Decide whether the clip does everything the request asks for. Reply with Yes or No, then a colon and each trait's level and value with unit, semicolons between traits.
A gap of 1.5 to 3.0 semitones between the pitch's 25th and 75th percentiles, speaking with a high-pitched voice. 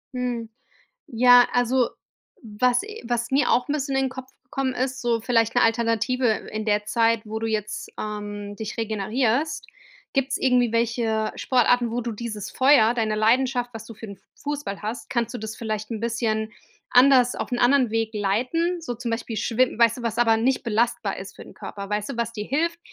Yes: narrow, 2.5 semitones; high, 235 Hz